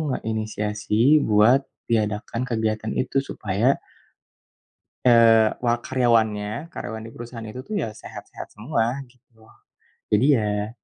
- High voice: No, low, 115 Hz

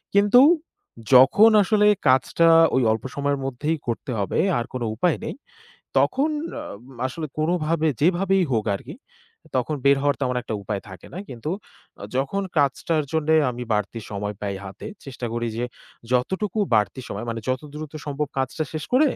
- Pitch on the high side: No, medium, 140 Hz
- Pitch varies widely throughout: Yes, wide, 5.7 semitones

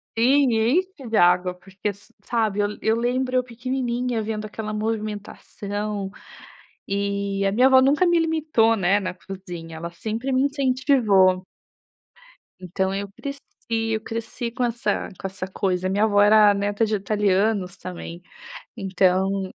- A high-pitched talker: Yes, high, 210 Hz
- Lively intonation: No, average, 3.7 semitones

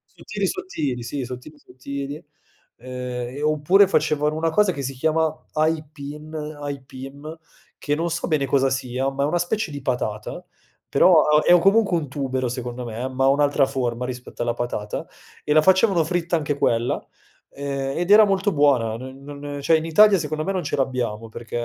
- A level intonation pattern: No, average, 3.7 semitones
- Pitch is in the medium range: Yes, medium, 145 Hz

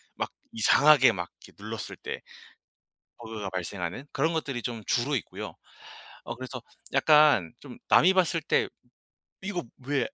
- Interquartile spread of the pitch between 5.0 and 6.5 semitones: Yes, wide, 5.6 semitones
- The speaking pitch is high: No, low, 130 Hz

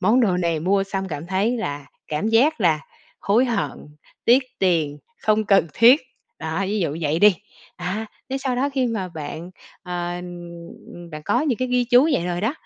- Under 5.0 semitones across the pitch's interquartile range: No, wide, 5.4 semitones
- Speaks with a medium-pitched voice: No, high, 195 Hz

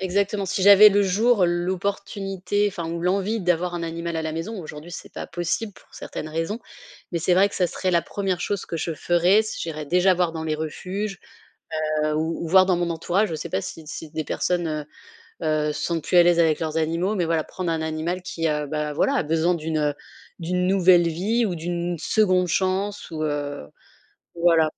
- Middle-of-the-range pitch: Yes, medium, 175 Hz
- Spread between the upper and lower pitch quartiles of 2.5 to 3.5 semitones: Yes, average, 2.9 semitones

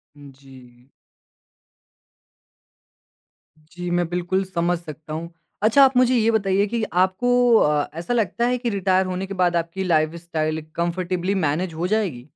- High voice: No, medium, 180 Hz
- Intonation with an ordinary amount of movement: Yes, average, 3.8 semitones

